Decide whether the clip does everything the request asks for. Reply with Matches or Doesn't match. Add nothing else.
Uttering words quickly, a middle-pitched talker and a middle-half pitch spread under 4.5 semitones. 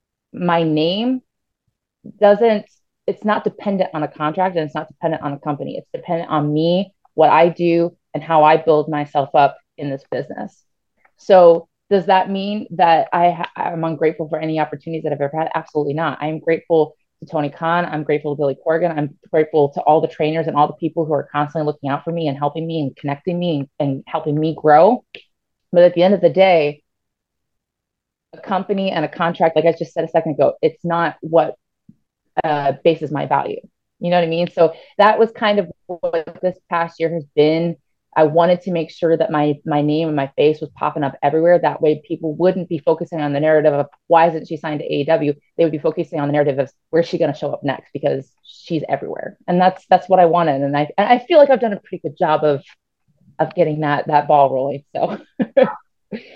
Matches